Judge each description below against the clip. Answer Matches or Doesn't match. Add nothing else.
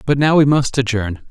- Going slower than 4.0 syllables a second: Doesn't match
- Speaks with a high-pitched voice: Doesn't match